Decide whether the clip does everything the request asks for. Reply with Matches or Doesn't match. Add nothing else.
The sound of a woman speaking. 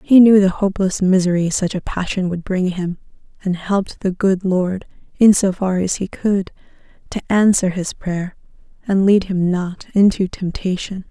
Matches